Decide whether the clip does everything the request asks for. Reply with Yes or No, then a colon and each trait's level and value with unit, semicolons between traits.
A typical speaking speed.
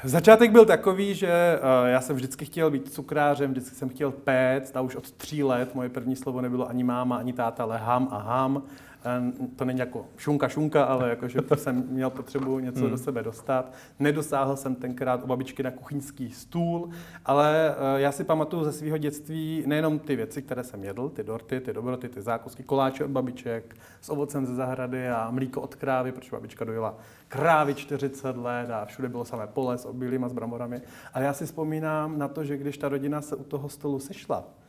No: fast, 195 wpm